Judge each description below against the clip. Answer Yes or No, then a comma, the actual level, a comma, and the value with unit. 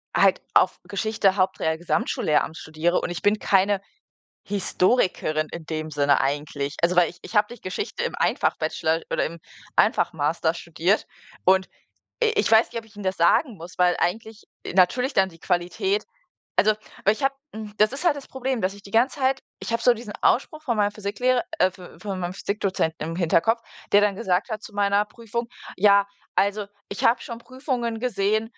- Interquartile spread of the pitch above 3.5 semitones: Yes, average, 4.5 semitones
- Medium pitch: No, high, 200 Hz